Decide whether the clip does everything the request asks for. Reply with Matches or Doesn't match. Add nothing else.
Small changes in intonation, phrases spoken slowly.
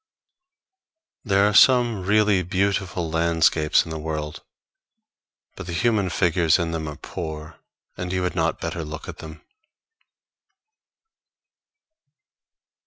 Doesn't match